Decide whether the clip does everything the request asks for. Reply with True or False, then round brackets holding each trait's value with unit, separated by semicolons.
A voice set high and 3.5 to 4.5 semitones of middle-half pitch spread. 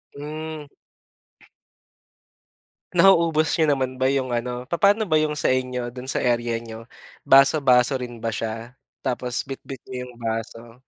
False (130 Hz; 3.9 semitones)